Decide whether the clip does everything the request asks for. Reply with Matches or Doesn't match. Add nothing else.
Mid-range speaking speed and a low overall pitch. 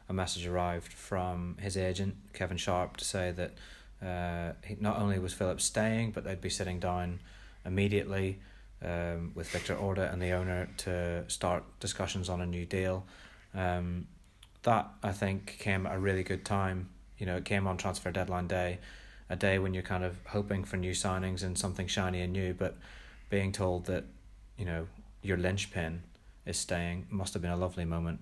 Matches